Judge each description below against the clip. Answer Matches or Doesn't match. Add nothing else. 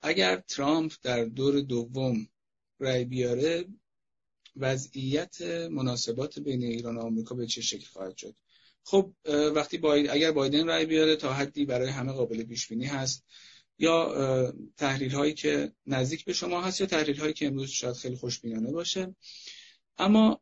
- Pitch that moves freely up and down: Doesn't match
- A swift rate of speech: Doesn't match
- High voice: Doesn't match